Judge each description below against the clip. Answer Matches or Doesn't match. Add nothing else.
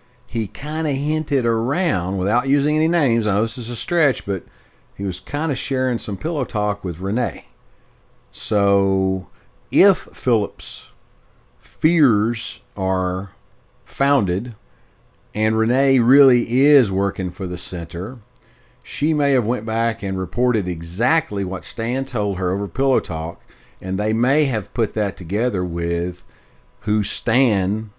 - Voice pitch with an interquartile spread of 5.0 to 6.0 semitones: Matches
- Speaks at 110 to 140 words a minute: Matches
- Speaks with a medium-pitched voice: Doesn't match